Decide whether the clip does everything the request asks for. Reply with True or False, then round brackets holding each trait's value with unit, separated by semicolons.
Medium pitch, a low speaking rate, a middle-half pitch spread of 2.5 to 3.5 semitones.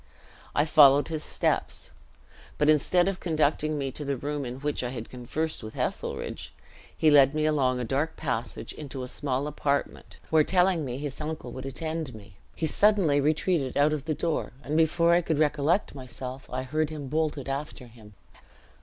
False (145 Hz; 185 wpm; 3.2 semitones)